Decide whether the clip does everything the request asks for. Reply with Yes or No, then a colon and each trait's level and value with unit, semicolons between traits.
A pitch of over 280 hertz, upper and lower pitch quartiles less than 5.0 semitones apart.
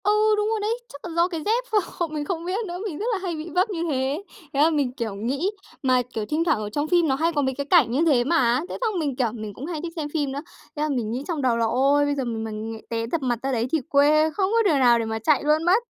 No: very high, 290 Hz; average, 5.3 semitones